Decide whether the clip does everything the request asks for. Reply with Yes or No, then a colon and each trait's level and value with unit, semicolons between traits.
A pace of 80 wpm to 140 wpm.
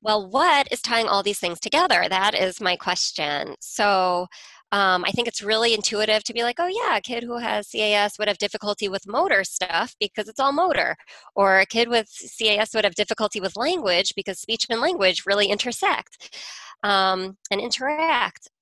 No: average, 185 wpm